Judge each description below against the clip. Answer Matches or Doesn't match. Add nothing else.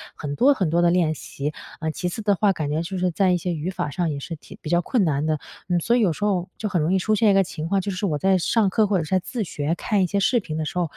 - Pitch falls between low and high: Matches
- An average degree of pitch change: Matches